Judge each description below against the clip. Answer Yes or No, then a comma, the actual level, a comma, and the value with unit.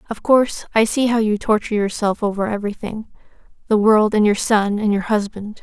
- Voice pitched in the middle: No, high, 215 Hz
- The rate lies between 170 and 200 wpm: Yes, average, 180 wpm